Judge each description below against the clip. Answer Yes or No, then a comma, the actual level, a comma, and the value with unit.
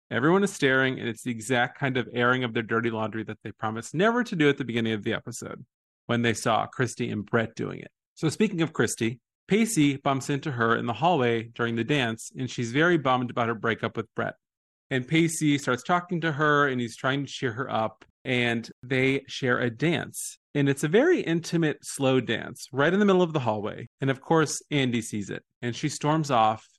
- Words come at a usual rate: No, fast, 220 wpm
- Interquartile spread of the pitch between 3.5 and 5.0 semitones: Yes, average, 4.5 semitones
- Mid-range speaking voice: No, low, 130 Hz